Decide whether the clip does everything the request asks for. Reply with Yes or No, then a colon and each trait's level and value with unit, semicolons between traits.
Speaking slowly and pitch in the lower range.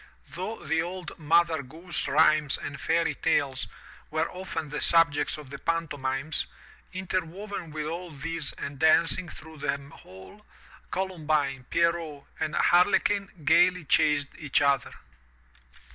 No: slow, 130 wpm; medium, 160 Hz